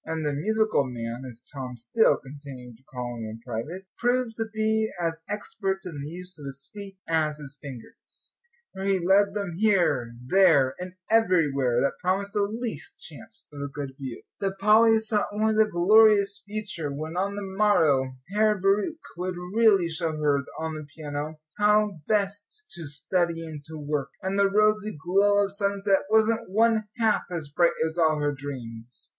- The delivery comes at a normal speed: Yes, average, 175 wpm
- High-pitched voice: No, medium, 180 Hz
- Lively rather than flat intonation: Yes, wide, 6.3 semitones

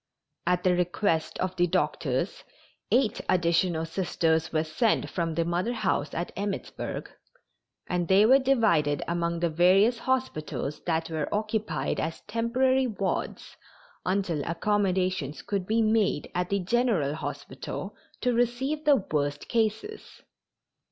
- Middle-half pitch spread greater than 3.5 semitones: Yes, average, 5.3 semitones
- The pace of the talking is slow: Yes, slow, 130 wpm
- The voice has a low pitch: No, medium, 185 Hz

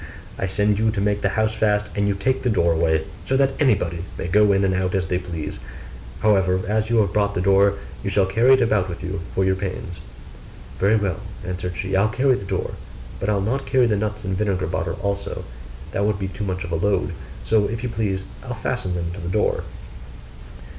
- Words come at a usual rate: No, fast, 225 wpm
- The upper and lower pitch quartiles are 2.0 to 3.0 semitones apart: Yes, narrow, 2.4 semitones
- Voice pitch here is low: Yes, low, 100 Hz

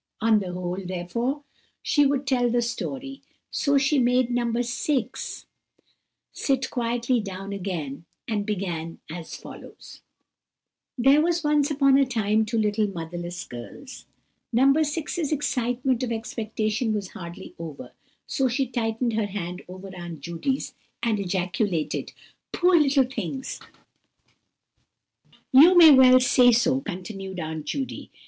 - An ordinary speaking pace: No, slow, 130 wpm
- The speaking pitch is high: Yes, high, 230 Hz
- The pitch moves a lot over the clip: Yes, wide, 6.1 semitones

